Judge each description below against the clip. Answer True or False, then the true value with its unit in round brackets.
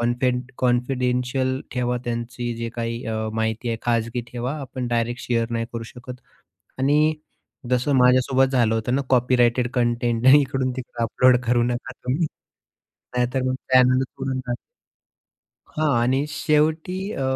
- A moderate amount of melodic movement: False (1.6 semitones)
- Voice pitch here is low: True (125 Hz)